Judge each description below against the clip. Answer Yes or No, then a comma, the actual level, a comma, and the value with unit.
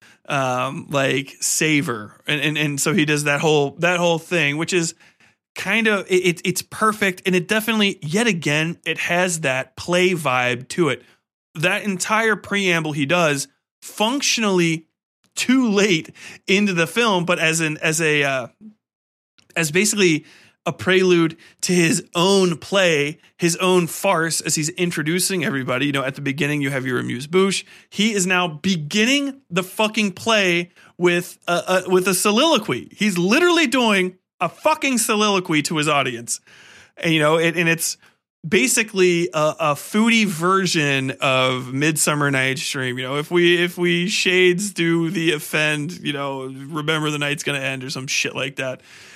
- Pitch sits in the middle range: Yes, medium, 170 Hz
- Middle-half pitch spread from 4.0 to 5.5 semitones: Yes, average, 4.4 semitones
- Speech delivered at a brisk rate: No, average, 165 wpm